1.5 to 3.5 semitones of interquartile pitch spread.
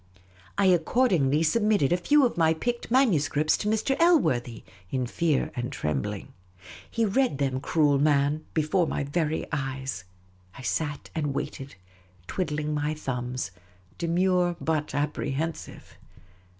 No: average, 4.6 semitones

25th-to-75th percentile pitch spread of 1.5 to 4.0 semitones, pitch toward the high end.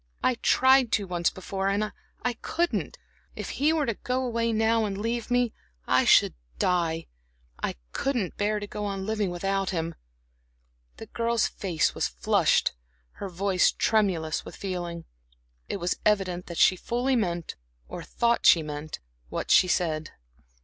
No: average, 4.7 semitones; high, 200 Hz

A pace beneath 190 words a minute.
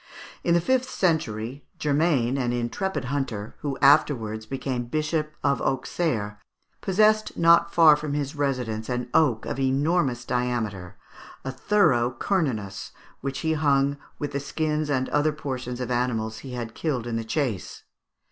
Yes: average, 145 wpm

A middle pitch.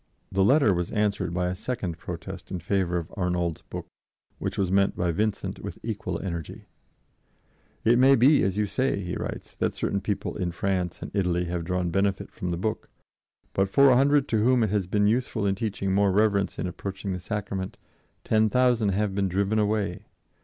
No: low, 100 Hz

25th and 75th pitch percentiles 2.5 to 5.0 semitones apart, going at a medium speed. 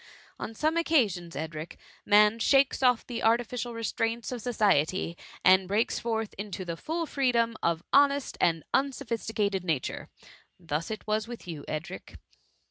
No: wide, 5.4 semitones; average, 150 wpm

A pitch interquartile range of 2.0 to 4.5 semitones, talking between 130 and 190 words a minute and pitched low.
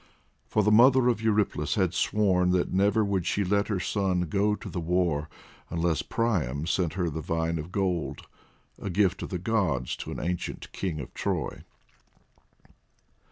Yes: average, 3.8 semitones; average, 165 wpm; very low, 90 Hz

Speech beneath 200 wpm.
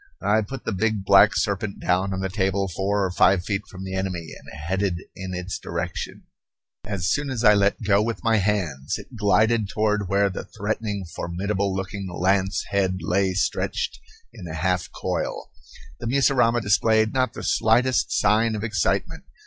Yes: average, 175 wpm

